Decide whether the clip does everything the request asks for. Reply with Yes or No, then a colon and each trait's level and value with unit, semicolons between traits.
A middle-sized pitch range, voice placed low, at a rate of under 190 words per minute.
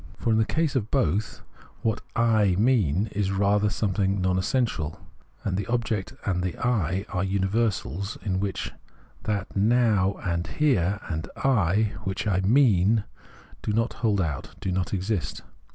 Yes: average, 3.2 semitones; low, 100 Hz; average, 150 wpm